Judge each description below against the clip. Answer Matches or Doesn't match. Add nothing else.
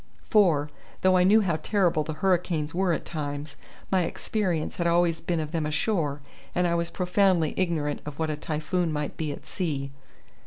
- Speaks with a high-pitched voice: Doesn't match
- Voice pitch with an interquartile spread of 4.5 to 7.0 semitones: Doesn't match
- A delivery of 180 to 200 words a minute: Matches